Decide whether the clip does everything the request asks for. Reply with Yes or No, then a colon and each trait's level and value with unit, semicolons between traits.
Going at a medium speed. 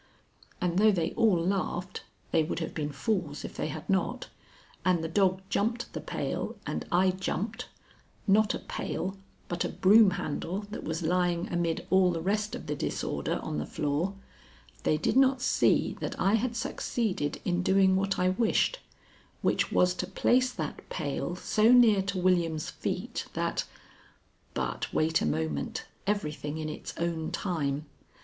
Yes: average, 165 wpm